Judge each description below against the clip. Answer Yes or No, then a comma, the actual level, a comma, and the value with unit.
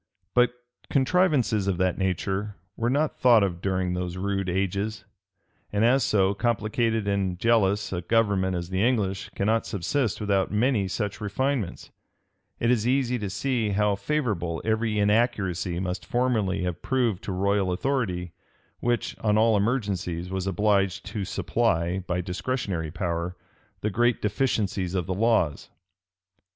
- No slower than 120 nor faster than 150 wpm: Yes, average, 140 wpm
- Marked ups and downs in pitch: No, average, 3.8 semitones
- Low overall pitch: Yes, low, 100 Hz